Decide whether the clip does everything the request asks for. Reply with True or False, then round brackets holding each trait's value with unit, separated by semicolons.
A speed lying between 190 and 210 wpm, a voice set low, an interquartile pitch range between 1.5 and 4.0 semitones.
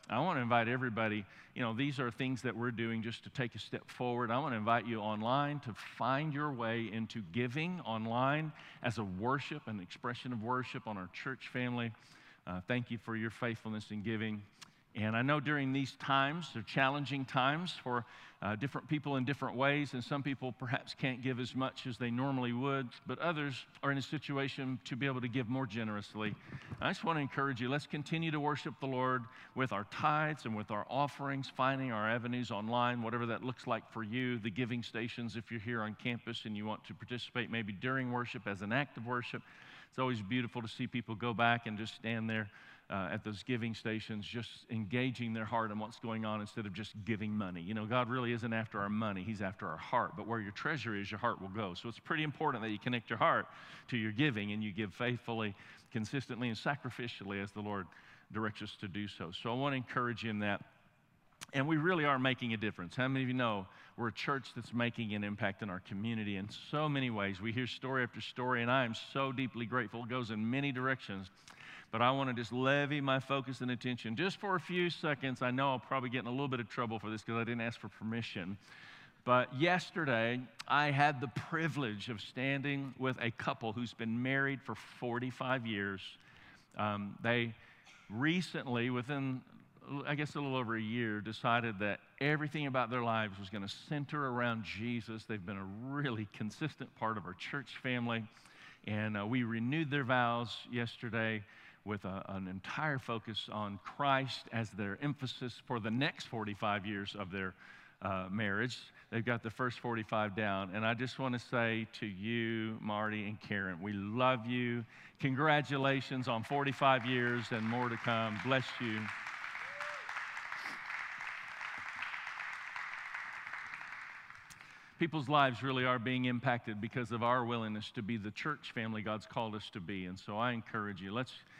True (200 wpm; 120 Hz; 3.3 semitones)